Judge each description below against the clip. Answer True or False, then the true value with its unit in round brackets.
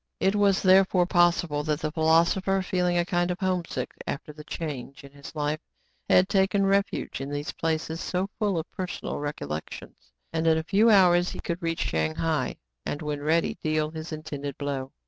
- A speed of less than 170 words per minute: False (185 wpm)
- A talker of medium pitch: True (165 Hz)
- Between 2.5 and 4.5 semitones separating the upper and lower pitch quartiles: True (3.6 semitones)